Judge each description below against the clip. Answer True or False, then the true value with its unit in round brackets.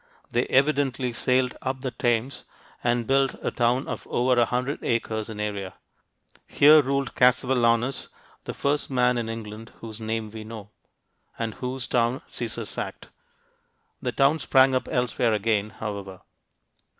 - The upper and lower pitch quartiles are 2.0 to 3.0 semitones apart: True (2.7 semitones)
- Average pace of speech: True (145 wpm)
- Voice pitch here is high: False (120 Hz)